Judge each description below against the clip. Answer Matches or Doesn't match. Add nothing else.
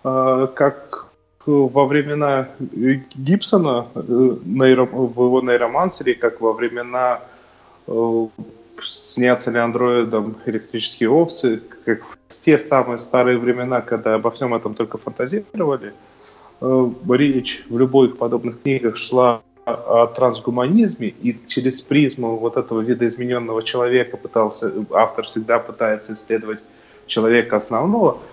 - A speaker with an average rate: Doesn't match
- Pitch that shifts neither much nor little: Doesn't match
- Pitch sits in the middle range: Doesn't match